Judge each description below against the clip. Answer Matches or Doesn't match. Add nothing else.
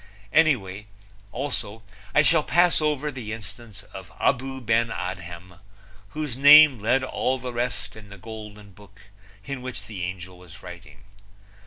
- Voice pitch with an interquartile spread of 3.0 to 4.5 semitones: Doesn't match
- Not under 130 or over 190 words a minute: Matches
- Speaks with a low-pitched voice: Matches